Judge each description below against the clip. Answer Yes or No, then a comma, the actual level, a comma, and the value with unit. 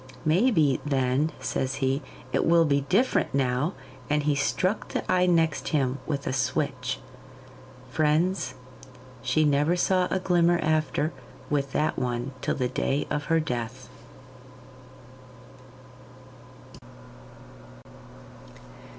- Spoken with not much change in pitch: No, average, 3.8 semitones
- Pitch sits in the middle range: Yes, medium, 145 Hz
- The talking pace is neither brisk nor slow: No, slow, 110 wpm